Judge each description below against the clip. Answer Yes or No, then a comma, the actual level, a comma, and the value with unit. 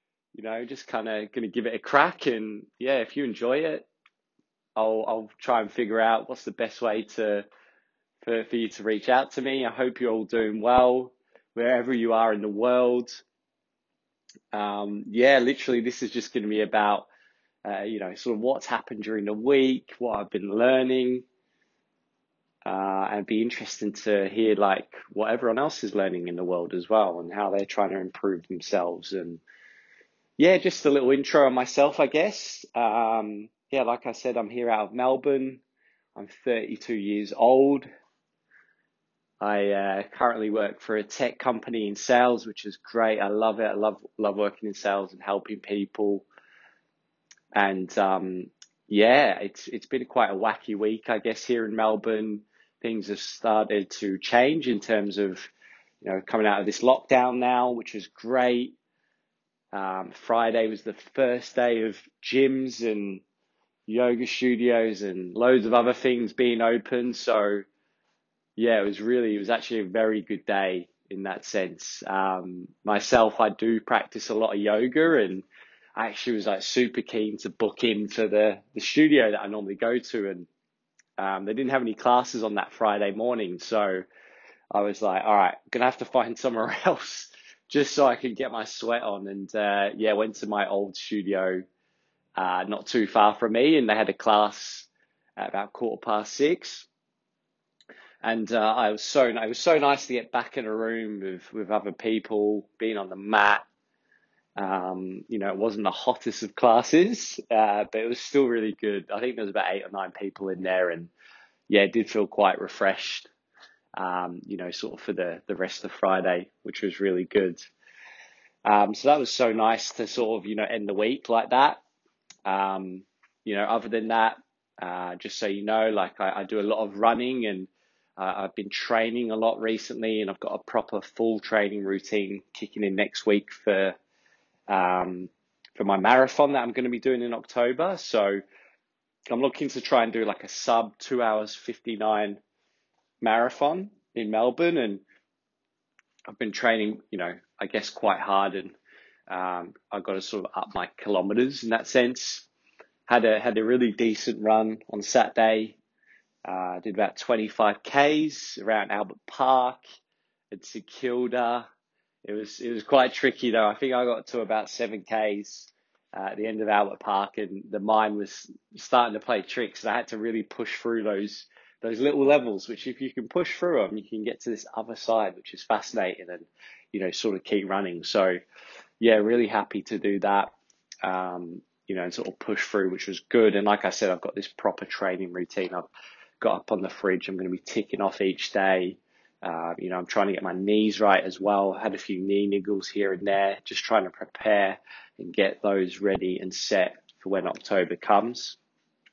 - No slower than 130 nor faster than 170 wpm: No, average, 190 wpm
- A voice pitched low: Yes, low, 110 Hz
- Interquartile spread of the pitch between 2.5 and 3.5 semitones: Yes, average, 3.0 semitones